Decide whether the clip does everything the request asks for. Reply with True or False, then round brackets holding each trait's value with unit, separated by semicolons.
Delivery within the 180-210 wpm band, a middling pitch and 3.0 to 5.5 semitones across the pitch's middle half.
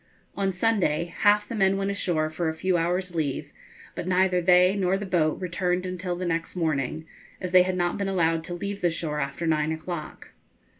False (200 wpm; 180 Hz; 2.6 semitones)